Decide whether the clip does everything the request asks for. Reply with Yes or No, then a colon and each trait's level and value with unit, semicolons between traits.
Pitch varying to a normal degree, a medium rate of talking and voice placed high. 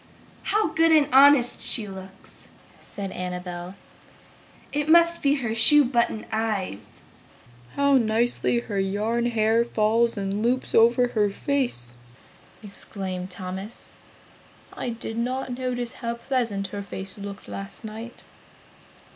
No: average, 4.0 semitones; slow, 120 wpm; high, 225 Hz